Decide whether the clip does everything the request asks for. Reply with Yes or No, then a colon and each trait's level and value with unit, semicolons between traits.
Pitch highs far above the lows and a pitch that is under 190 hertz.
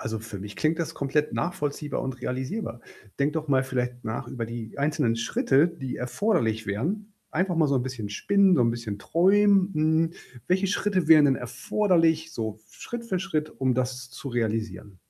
Yes: wide, 6.2 semitones; medium, 140 Hz